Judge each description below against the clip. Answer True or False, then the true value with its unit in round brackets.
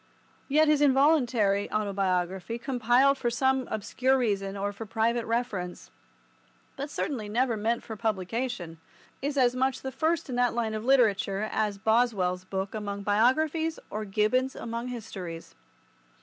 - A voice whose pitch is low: False (230 Hz)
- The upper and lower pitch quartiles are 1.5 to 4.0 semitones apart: False (4.4 semitones)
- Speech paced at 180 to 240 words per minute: False (140 wpm)